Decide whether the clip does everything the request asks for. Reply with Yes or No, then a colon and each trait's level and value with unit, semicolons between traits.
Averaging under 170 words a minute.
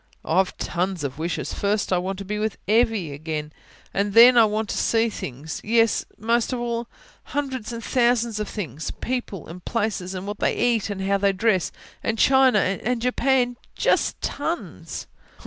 No: average, 185 wpm